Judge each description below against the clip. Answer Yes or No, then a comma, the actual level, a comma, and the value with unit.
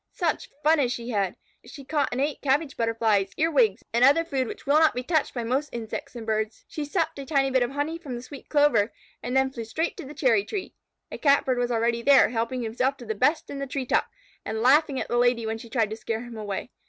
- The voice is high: Yes, very high, 255 Hz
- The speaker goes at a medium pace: No, fast, 250 wpm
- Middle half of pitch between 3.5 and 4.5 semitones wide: Yes, average, 3.9 semitones